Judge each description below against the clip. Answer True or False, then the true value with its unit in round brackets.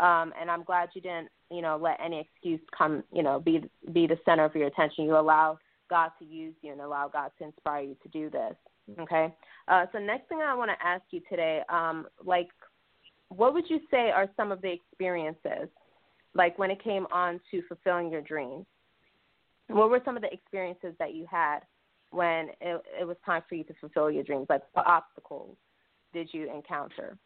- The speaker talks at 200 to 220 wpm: True (205 wpm)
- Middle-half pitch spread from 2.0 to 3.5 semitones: True (2.7 semitones)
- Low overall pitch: False (170 Hz)